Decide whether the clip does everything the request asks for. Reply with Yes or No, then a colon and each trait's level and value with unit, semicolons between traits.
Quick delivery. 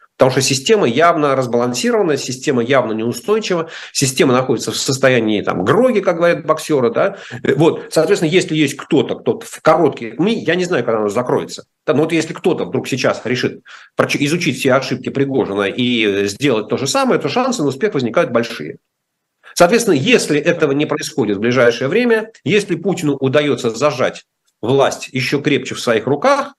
Yes: fast, 165 wpm